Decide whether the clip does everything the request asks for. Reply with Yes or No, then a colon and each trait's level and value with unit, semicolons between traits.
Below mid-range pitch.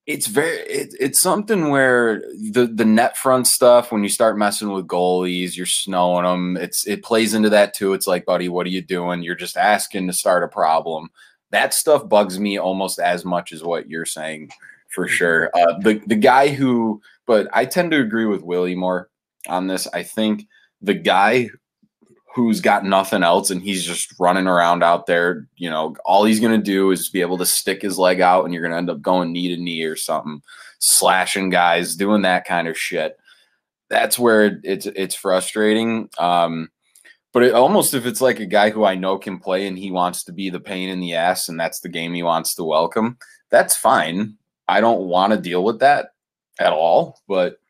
Yes: very low, 95 Hz